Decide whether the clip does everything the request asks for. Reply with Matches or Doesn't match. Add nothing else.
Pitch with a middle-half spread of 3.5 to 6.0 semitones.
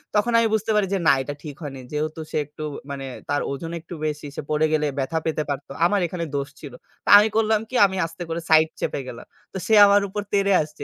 Matches